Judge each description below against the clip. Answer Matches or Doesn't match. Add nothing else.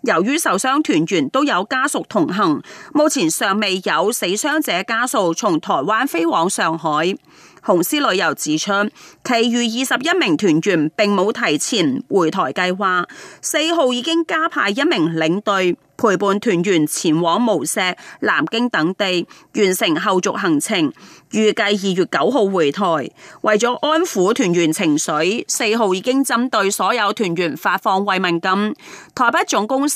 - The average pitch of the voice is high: Matches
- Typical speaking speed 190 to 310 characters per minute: Matches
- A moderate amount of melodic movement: Doesn't match